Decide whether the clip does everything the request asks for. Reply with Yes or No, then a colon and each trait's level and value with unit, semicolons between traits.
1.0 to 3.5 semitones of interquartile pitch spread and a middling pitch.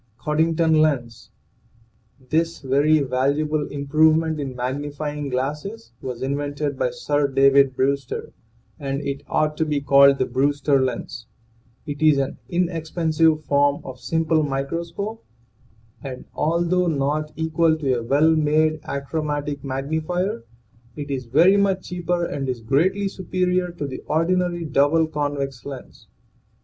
Yes: average, 2.8 semitones; medium, 150 Hz